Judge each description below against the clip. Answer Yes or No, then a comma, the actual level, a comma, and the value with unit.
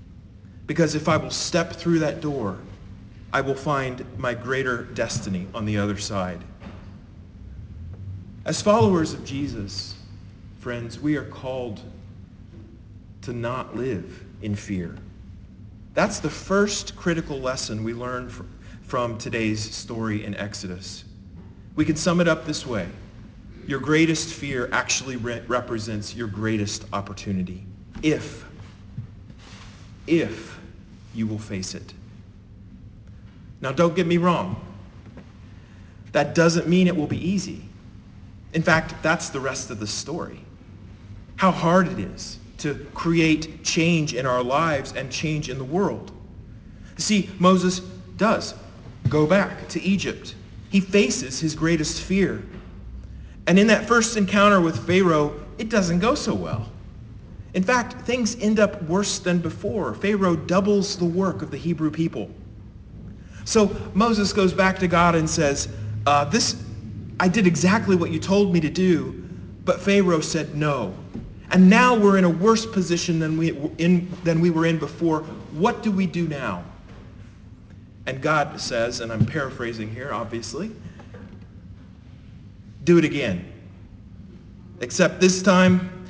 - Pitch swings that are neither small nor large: No, wide, 8.7 semitones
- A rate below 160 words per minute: Yes, average, 140 wpm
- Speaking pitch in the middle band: No, low, 125 Hz